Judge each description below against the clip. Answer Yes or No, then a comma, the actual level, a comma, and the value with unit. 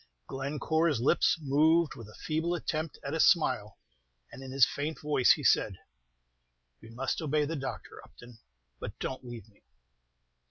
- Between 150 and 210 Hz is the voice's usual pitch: No, medium, 140 Hz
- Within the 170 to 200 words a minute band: No, average, 155 wpm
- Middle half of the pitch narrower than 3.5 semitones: No, average, 4.1 semitones